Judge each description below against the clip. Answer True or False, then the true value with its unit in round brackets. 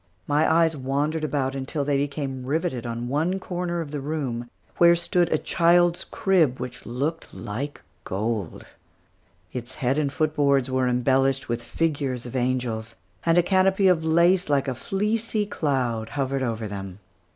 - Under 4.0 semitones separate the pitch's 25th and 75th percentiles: False (4.7 semitones)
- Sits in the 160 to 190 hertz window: False (140 Hz)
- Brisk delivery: False (160 wpm)